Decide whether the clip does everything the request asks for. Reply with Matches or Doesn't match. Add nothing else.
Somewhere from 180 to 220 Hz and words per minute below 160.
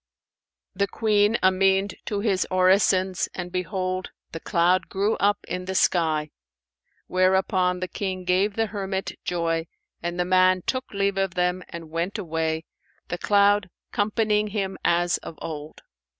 Matches